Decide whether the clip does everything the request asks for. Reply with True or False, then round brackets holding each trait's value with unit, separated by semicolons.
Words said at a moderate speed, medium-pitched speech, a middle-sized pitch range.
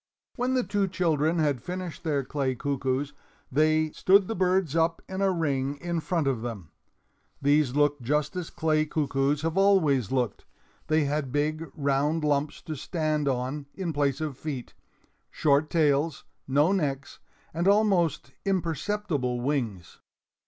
True (145 wpm; 150 Hz; 3.4 semitones)